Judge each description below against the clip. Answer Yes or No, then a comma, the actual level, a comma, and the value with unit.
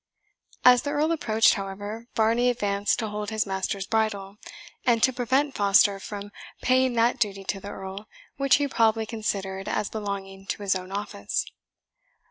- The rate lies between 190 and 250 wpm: No, average, 160 wpm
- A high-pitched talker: Yes, high, 210 Hz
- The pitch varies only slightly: No, average, 3.2 semitones